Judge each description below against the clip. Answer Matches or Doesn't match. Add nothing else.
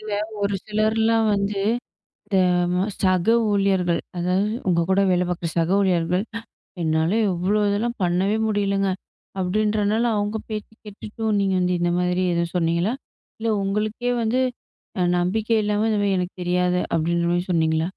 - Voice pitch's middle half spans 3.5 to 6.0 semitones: Doesn't match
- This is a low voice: Doesn't match